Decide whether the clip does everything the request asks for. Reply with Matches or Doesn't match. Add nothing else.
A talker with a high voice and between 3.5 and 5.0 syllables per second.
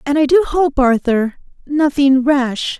Matches